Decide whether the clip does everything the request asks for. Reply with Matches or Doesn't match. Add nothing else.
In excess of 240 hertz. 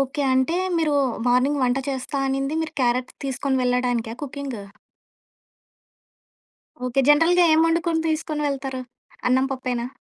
Matches